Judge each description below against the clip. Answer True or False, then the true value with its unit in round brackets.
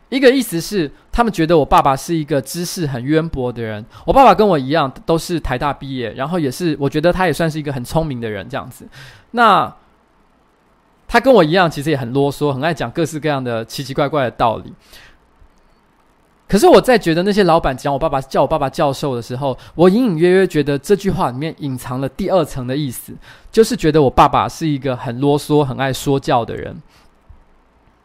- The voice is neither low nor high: True (150 Hz)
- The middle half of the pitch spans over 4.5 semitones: False (4.2 semitones)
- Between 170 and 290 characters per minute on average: False (310 characters per minute)